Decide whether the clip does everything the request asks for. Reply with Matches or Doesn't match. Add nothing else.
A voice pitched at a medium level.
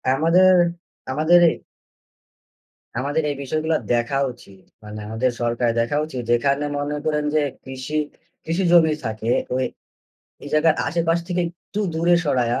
Matches